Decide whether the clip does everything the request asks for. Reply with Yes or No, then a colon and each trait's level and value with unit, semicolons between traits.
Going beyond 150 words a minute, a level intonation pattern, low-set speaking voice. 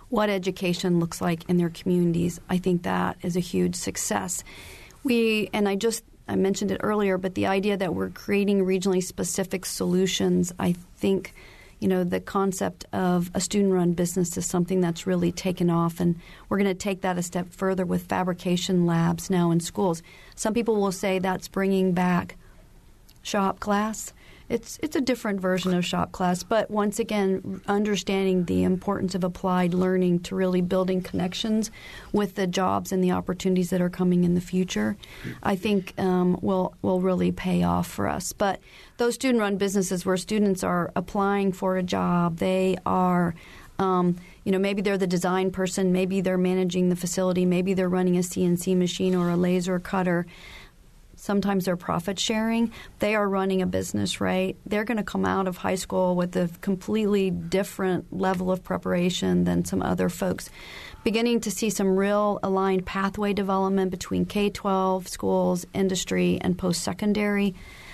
No: average, 175 wpm; narrow, 1.7 semitones; medium, 185 Hz